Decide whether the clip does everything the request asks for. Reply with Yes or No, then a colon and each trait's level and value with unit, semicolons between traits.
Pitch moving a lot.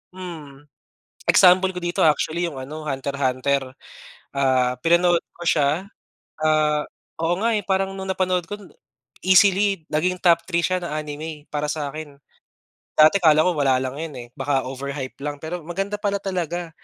No: average, 4.1 semitones